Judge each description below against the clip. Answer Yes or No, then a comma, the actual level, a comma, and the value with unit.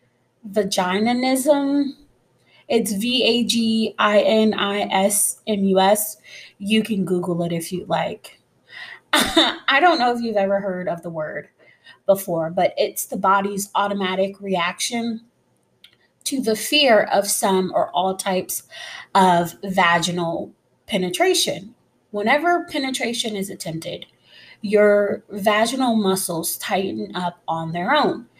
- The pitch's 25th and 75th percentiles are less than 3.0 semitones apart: No, average, 3.8 semitones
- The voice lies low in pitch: No, high, 200 Hz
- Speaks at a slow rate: Yes, slow, 105 wpm